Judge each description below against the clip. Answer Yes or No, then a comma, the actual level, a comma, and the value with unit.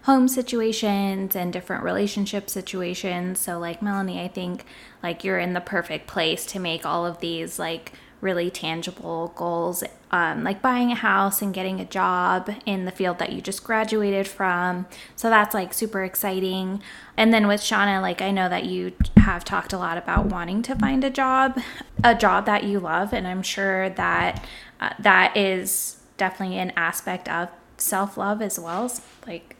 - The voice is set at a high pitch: Yes, high, 195 Hz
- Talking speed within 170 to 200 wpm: Yes, average, 180 wpm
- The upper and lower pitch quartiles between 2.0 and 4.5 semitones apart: Yes, average, 2.7 semitones